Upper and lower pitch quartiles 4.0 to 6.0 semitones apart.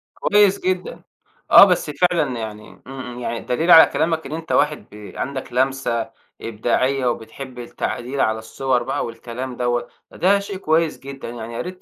Yes: average, 5.2 semitones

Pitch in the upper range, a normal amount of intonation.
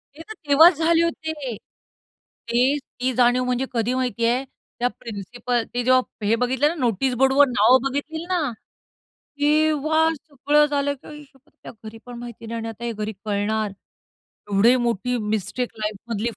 Yes: very high, 255 Hz; average, 4.0 semitones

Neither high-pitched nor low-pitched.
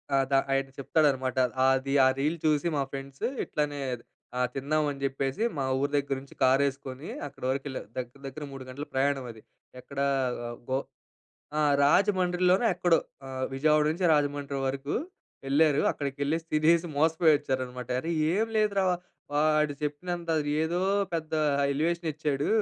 Yes: medium, 145 Hz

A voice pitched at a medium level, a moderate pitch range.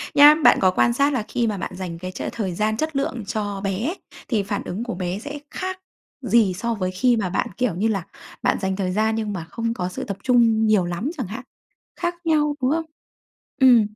No: high, 220 Hz; average, 4.9 semitones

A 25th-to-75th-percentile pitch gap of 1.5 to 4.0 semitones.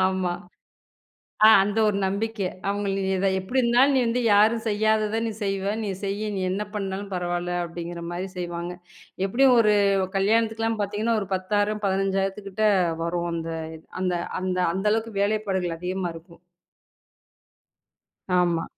Yes: average, 2.9 semitones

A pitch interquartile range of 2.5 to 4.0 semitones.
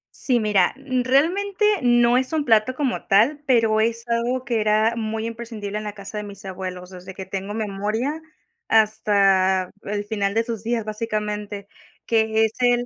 Yes: average, 2.8 semitones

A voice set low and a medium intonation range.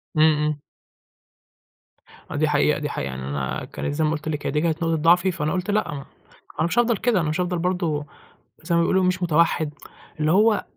No: medium, 160 Hz; average, 3.2 semitones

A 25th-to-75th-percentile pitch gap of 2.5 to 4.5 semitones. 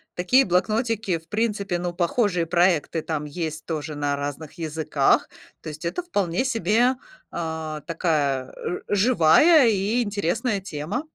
No: average, 5.2 semitones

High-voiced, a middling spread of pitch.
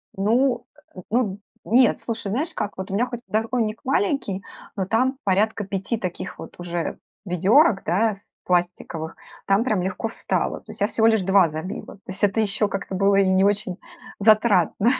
Yes: high, 205 Hz; average, 3.2 semitones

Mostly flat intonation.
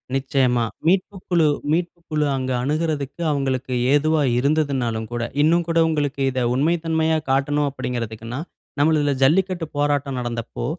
No: average, 3.6 semitones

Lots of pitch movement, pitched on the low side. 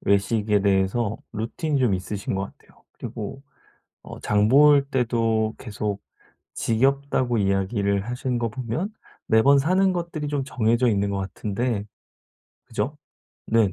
No: average, 4.7 semitones; low, 115 Hz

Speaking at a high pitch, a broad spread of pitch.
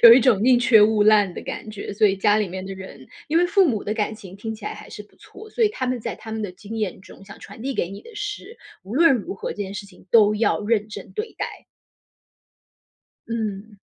No: high, 215 Hz; average, 3.4 semitones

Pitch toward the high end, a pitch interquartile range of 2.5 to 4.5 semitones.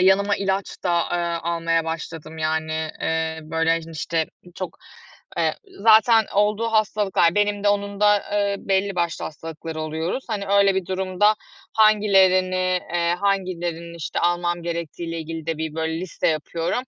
No: medium, 175 Hz; average, 3.6 semitones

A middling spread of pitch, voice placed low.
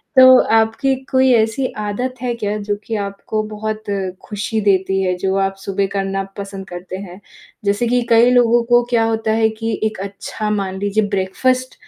No: average, 3.0 semitones; high, 215 Hz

